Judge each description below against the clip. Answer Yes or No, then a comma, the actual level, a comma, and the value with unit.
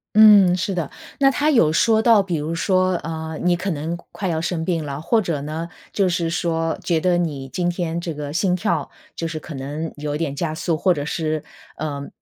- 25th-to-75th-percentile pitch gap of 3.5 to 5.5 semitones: No, average, 2.8 semitones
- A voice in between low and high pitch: Yes, medium, 165 Hz